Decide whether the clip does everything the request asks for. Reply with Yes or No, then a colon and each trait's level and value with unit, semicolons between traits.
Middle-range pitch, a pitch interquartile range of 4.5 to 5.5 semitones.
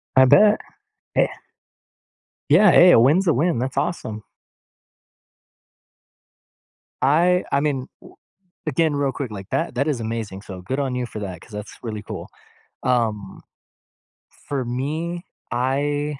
No: low, 130 Hz; average, 4.9 semitones